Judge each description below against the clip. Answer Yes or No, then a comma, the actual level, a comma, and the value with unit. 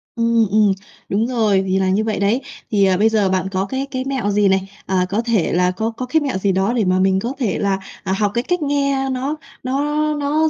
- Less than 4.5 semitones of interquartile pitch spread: No, average, 5.1 semitones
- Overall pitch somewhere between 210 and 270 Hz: Yes, high, 215 Hz